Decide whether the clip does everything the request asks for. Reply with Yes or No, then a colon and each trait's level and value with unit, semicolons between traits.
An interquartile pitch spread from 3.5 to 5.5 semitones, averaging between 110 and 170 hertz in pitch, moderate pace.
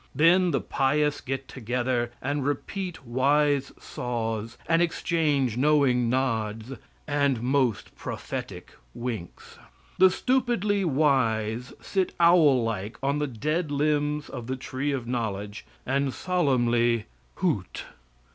No: average, 4.0 semitones; low, 135 Hz; slow, 115 wpm